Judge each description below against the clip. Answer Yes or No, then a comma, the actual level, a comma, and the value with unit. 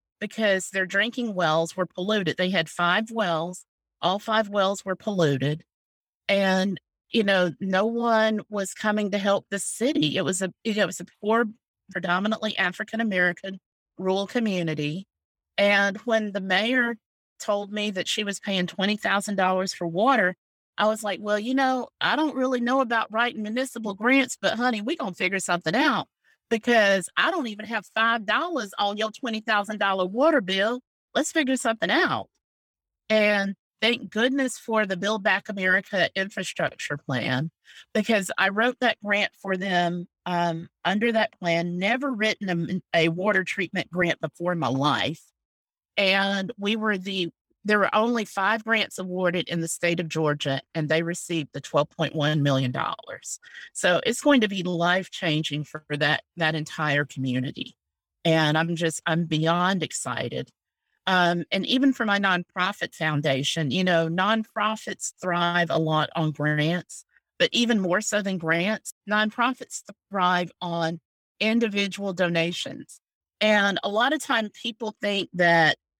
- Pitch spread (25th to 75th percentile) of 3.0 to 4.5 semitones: Yes, average, 4.1 semitones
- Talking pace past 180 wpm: No, average, 155 wpm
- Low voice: No, high, 195 Hz